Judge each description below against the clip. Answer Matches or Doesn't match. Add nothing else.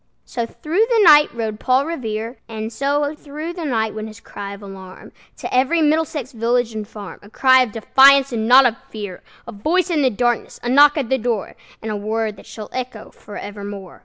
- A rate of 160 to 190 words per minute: Doesn't match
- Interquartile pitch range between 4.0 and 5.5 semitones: Matches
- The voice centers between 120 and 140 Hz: Doesn't match